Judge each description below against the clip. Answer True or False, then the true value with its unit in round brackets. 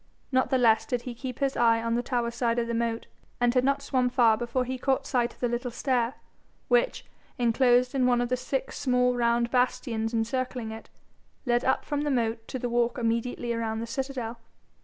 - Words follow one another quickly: True (210 wpm)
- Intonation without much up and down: True (1.7 semitones)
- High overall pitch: True (245 Hz)